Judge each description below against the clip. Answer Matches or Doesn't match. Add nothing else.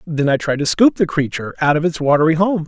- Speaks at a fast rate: Matches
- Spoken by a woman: Doesn't match